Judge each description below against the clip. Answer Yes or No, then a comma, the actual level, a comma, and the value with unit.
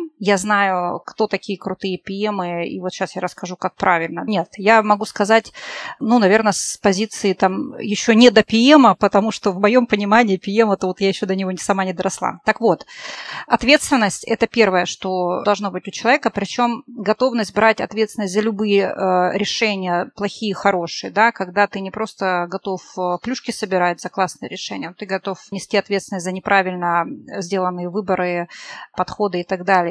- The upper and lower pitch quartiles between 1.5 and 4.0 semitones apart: Yes, average, 2.8 semitones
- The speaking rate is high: Yes, fast, 170 wpm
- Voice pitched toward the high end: Yes, high, 200 Hz